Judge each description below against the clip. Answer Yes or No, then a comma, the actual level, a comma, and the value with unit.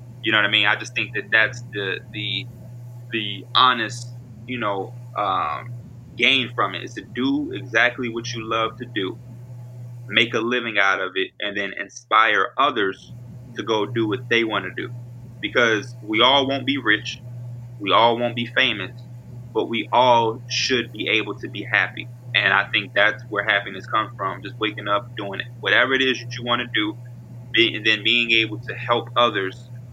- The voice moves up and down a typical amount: No, narrow, 1.6 semitones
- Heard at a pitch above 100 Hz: Yes, low, 120 Hz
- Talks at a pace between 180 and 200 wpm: Yes, average, 190 wpm